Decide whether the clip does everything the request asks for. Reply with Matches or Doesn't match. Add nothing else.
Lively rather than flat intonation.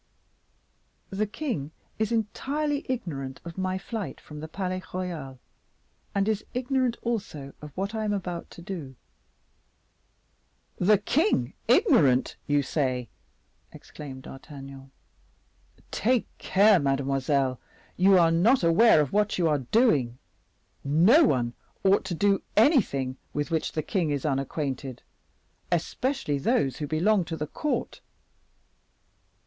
Matches